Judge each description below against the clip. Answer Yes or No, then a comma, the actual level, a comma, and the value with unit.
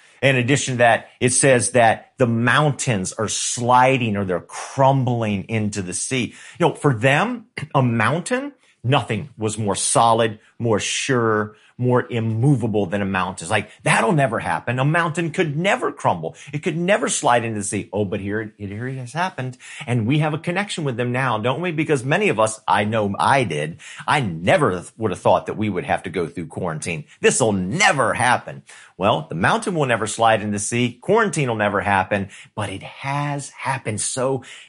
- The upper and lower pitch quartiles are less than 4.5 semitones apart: No, average, 5.0 semitones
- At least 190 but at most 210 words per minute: Yes, average, 195 wpm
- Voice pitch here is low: Yes, low, 125 Hz